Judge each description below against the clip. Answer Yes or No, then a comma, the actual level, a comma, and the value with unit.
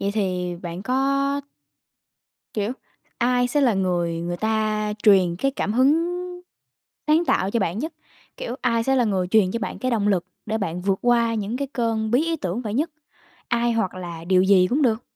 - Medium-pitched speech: No, high, 220 Hz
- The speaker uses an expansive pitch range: No, average, 4.8 semitones